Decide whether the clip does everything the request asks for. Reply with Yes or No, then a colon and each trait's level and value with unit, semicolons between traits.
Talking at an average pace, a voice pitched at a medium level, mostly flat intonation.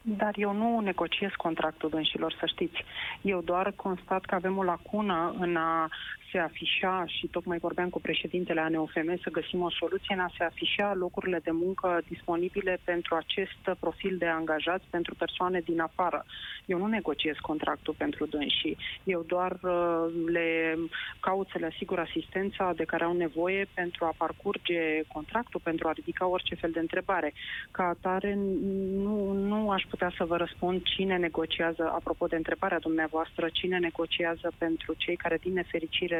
Yes: average, 160 wpm; medium, 175 Hz; narrow, 2.1 semitones